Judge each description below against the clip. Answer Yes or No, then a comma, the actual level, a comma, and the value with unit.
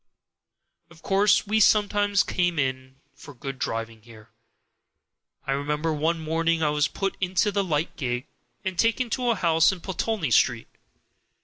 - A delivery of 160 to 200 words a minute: No, average, 150 wpm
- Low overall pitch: No, medium, 165 Hz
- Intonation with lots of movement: Yes, wide, 6.1 semitones